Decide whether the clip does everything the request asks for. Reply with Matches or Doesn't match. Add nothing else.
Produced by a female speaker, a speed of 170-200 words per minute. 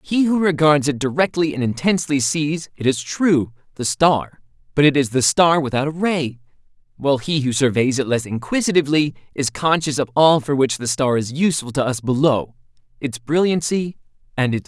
Doesn't match